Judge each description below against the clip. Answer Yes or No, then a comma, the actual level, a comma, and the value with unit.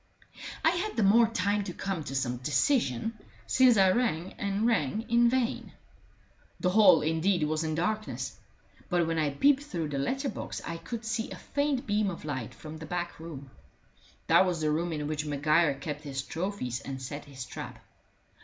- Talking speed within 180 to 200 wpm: Yes, average, 185 wpm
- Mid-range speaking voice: Yes, medium, 170 Hz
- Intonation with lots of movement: Yes, wide, 6.5 semitones